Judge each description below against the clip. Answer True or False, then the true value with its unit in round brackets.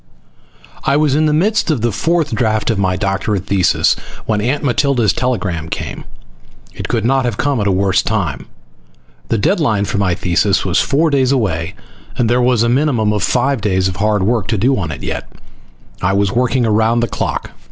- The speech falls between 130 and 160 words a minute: False (200 wpm)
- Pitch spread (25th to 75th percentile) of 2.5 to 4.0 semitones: False (4.8 semitones)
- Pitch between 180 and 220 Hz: False (110 Hz)